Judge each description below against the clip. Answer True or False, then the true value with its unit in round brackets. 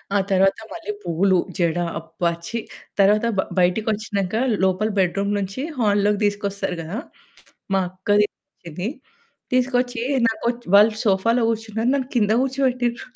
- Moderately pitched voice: False (210 Hz)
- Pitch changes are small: False (3.5 semitones)